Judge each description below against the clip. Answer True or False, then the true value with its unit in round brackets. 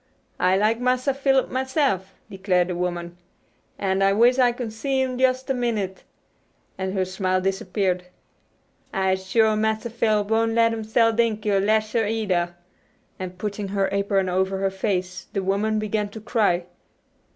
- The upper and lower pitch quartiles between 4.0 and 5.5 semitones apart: False (3.2 semitones)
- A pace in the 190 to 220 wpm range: False (165 wpm)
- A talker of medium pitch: False (205 Hz)